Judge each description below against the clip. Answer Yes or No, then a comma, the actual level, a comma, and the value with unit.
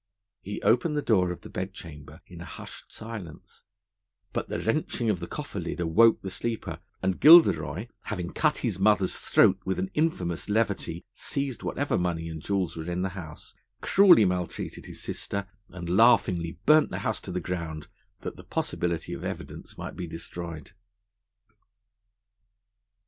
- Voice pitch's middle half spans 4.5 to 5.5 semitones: Yes, average, 4.8 semitones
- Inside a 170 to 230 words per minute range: No, average, 160 wpm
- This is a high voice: No, very low, 95 Hz